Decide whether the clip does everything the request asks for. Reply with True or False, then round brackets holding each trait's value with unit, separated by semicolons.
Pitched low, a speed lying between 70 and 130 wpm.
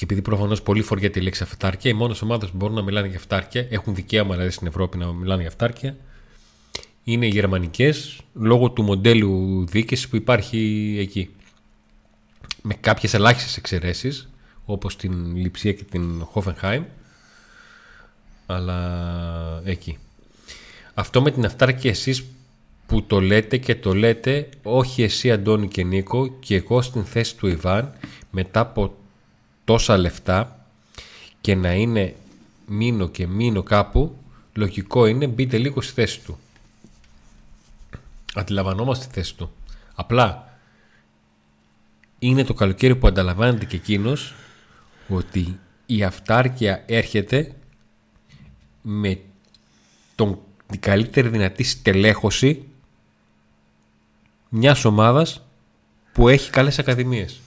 True (105 Hz; 120 wpm)